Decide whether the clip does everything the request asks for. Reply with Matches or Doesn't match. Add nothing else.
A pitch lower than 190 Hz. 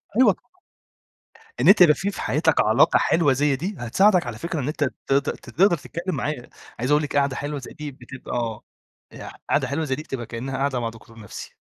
Matches